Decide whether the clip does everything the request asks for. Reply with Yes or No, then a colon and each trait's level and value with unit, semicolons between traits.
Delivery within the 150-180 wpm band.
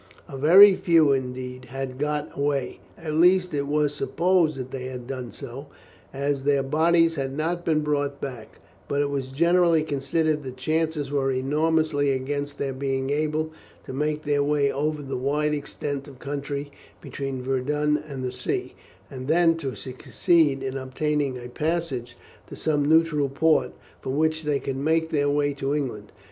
Yes: average, 170 wpm